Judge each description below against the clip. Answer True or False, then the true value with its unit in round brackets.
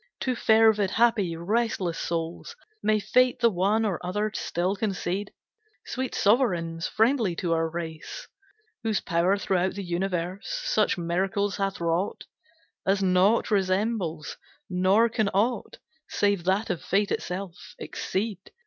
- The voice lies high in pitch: True (195 Hz)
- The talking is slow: True (130 wpm)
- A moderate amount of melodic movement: True (3.8 semitones)